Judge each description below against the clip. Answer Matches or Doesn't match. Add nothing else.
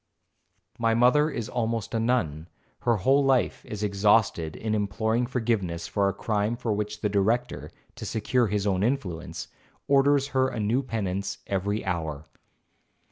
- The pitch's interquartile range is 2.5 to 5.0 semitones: Matches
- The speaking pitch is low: Matches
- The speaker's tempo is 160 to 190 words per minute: Doesn't match